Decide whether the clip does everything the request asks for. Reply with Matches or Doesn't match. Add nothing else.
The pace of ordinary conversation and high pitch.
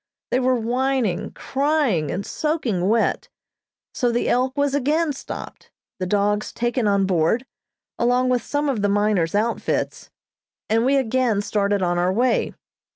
Matches